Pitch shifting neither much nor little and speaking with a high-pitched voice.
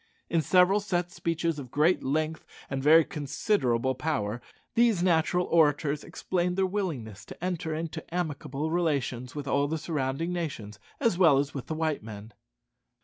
No: average, 4.3 semitones; medium, 155 Hz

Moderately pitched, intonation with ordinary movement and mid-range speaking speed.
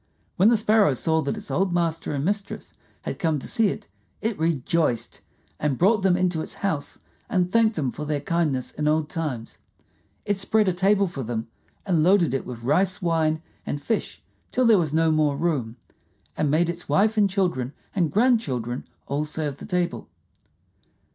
Yes: medium, 165 Hz; average, 4.9 semitones; average, 180 wpm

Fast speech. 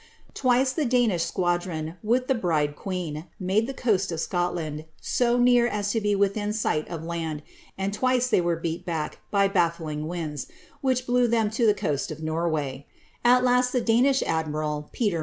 No: average, 175 wpm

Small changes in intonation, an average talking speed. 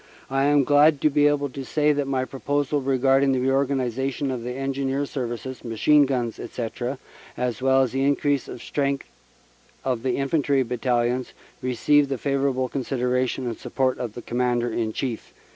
Yes: narrow, 2.0 semitones; average, 160 wpm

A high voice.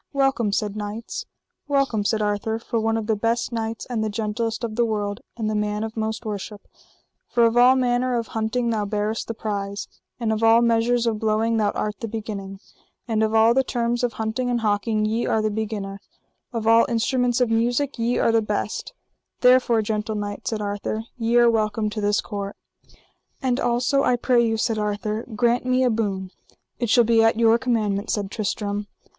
Yes: high, 225 Hz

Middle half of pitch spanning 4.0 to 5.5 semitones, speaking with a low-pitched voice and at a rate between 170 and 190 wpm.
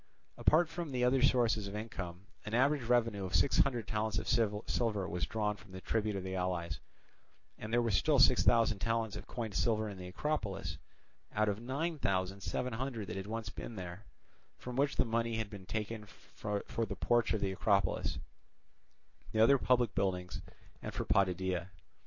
No: average, 3.6 semitones; low, 110 Hz; average, 180 wpm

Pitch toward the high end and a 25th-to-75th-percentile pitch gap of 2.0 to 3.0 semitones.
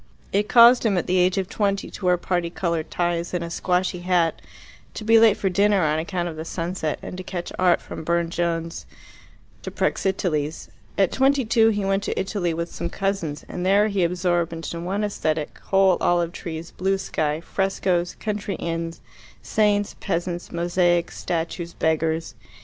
No: medium, 180 Hz; narrow, 2.5 semitones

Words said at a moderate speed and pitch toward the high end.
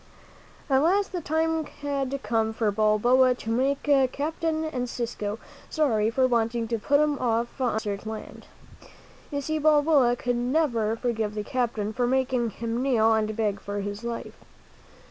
Yes: average, 160 wpm; high, 245 Hz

